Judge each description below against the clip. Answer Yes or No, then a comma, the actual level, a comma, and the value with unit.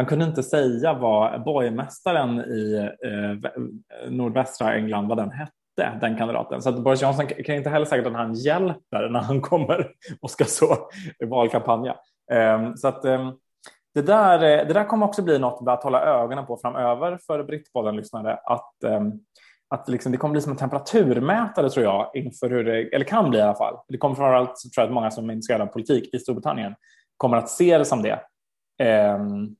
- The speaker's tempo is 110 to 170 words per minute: No, average, 200 wpm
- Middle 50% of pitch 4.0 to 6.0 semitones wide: Yes, average, 4.5 semitones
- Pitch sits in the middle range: No, low, 130 Hz